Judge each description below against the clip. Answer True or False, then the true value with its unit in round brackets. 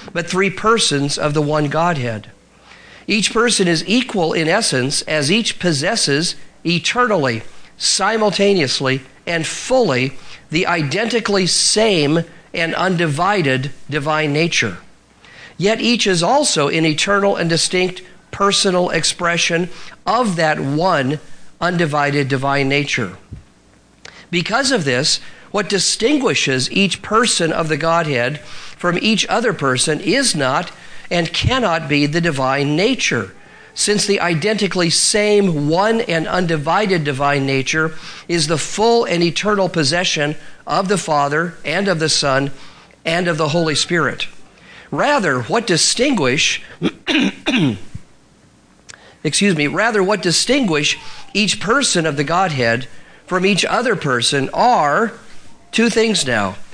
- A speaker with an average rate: False (120 wpm)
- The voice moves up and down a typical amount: True (5.0 semitones)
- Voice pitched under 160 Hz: False (170 Hz)